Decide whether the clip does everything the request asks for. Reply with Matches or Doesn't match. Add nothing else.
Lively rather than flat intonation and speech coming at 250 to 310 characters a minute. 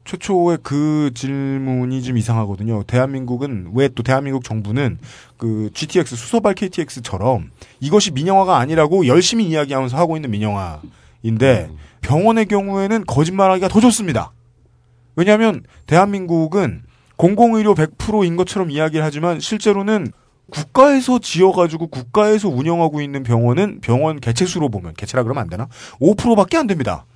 Doesn't match